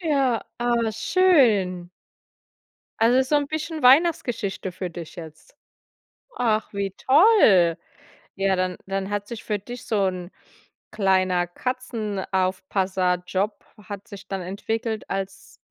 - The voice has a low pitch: No, high, 200 Hz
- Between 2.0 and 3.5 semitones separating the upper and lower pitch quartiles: No, average, 4.5 semitones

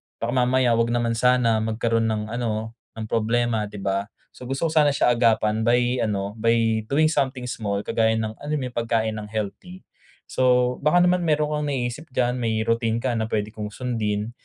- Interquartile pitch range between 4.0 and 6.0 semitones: No, narrow, 2.4 semitones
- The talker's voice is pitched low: Yes, low, 115 Hz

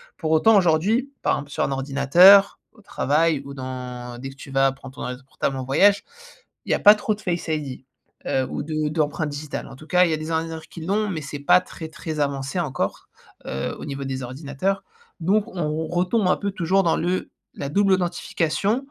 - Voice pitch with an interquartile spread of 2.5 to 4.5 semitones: No, average, 5.0 semitones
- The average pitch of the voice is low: No, medium, 155 Hz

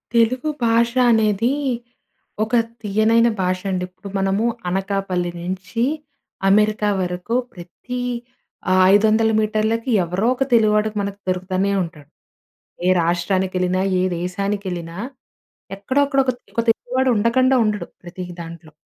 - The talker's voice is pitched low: No, high, 200 Hz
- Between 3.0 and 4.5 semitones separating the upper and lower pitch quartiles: Yes, average, 3.7 semitones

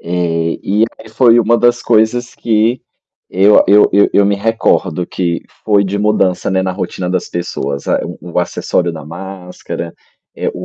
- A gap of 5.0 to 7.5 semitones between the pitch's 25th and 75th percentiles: No, average, 3.7 semitones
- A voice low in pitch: Yes, very low, 95 Hz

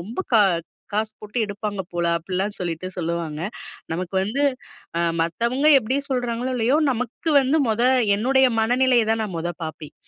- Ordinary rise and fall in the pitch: No, wide, 5.9 semitones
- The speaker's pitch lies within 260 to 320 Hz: No, high, 215 Hz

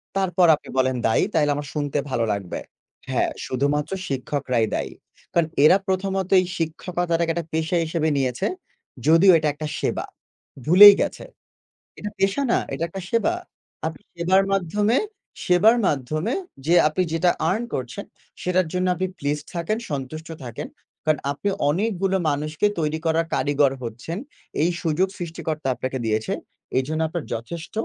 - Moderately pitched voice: Yes, medium, 160 Hz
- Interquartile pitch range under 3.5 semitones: No, average, 4.1 semitones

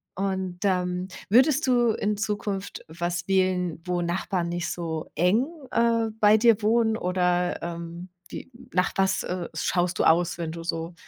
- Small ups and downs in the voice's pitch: No, average, 3.3 semitones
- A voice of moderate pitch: Yes, medium, 180 Hz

